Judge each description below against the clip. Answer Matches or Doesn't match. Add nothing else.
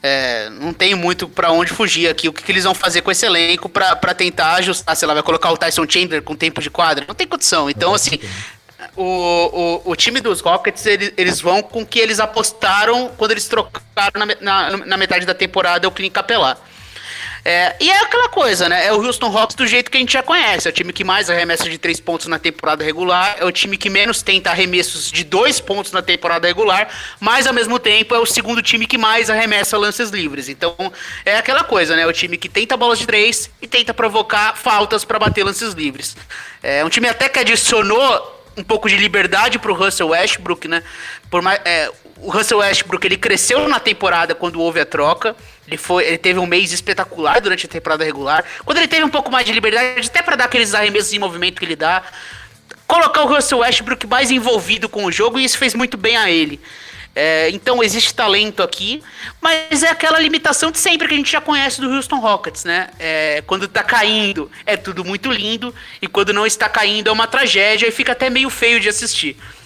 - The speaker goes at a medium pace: Doesn't match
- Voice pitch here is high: Matches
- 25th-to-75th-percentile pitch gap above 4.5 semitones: Matches